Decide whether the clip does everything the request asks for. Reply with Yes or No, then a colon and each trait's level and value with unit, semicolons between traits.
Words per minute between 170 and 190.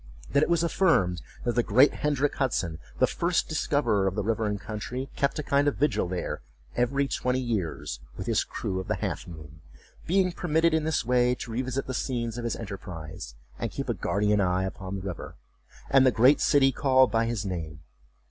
No: average, 200 wpm